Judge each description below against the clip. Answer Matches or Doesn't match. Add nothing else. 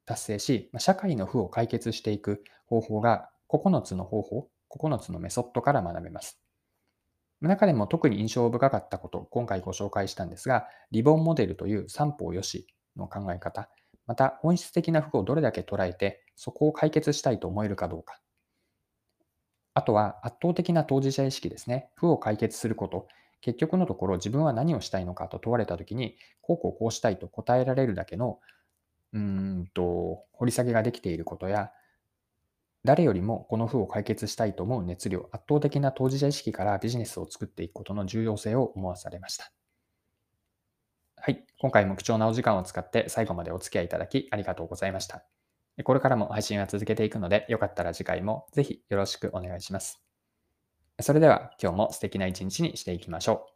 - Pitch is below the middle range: Matches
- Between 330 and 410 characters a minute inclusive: Matches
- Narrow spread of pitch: Doesn't match